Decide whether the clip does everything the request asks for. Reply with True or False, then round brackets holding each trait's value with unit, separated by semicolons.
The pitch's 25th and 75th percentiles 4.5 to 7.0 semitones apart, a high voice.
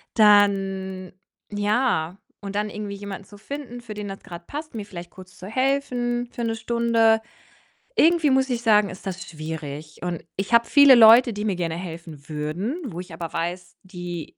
True (4.9 semitones; 205 Hz)